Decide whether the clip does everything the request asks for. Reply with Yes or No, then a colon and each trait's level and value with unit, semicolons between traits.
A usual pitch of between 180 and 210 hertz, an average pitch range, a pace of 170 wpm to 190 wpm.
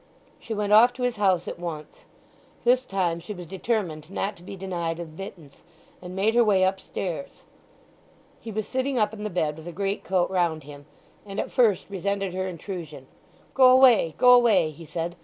Yes: high, 190 Hz; average, 4.0 semitones; average, 180 wpm